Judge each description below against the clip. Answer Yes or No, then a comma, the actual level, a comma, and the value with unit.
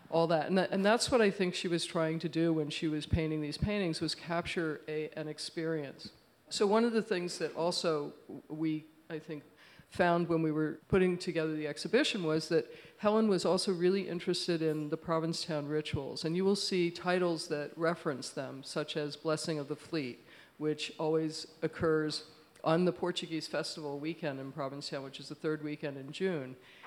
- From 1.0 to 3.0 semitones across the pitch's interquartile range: Yes, narrow, 2.4 semitones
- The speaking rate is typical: Yes, average, 190 wpm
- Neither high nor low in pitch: Yes, medium, 160 Hz